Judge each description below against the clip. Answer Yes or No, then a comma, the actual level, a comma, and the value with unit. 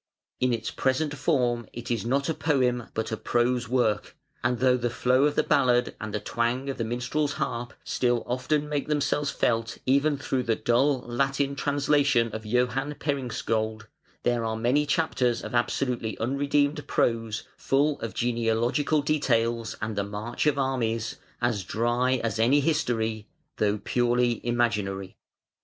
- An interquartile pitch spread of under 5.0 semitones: Yes, average, 3.2 semitones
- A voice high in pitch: No, low, 120 Hz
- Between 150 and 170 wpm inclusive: Yes, average, 155 wpm